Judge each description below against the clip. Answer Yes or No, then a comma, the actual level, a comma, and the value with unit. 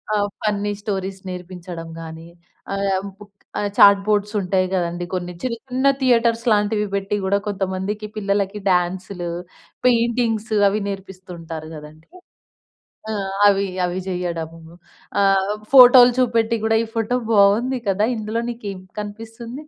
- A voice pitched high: Yes, high, 200 Hz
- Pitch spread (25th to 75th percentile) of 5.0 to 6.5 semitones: No, average, 3.2 semitones